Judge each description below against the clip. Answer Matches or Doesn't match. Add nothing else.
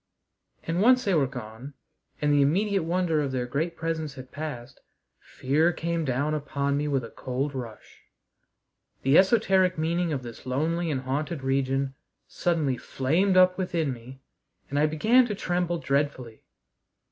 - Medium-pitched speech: Matches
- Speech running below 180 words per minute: Matches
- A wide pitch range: Doesn't match